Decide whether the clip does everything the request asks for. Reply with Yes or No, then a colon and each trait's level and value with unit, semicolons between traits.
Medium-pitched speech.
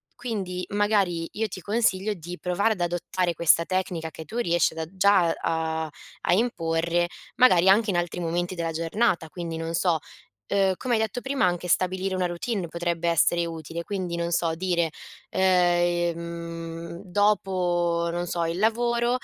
Yes: medium, 175 Hz